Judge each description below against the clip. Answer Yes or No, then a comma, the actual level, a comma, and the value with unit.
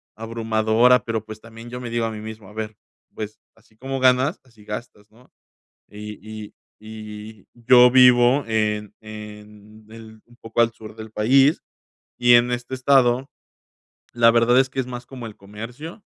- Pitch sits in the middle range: No, low, 115 Hz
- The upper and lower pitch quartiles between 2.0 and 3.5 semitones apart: Yes, narrow, 2.4 semitones